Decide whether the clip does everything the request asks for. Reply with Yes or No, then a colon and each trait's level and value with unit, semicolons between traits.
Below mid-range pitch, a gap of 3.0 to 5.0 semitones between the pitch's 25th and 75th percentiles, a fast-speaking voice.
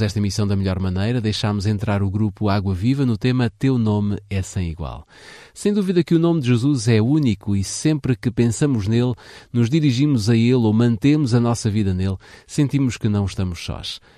Yes: low, 115 Hz; average, 4.1 semitones; fast, 200 wpm